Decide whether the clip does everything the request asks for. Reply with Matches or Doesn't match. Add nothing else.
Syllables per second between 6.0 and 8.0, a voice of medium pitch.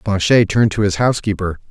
Doesn't match